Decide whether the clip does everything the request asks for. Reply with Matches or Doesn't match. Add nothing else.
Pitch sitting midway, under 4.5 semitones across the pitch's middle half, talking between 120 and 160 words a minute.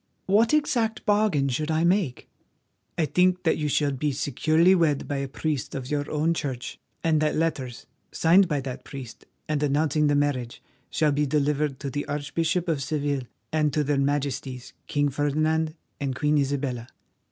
Doesn't match